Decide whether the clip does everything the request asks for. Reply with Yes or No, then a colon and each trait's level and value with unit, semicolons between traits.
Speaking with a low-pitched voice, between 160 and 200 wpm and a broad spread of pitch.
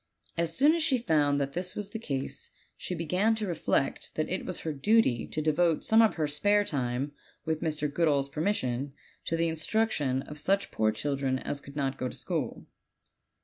No: medium, 155 Hz; average, 190 wpm; wide, 5.8 semitones